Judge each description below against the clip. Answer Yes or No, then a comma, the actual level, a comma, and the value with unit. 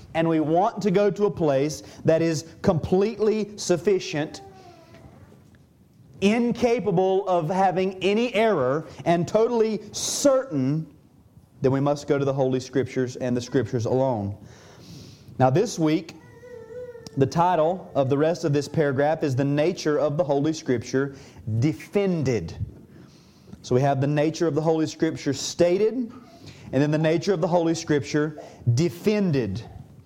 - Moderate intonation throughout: No, wide, 5.8 semitones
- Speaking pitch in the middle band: Yes, medium, 155 Hz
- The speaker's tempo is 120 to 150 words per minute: Yes, average, 140 wpm